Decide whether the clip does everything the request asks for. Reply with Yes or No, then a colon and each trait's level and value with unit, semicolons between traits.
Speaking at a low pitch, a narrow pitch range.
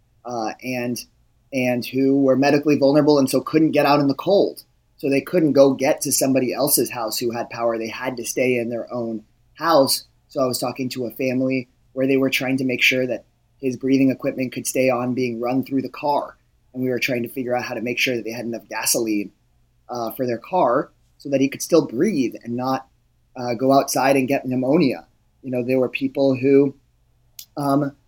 Yes: low, 130 Hz; narrow, 2.1 semitones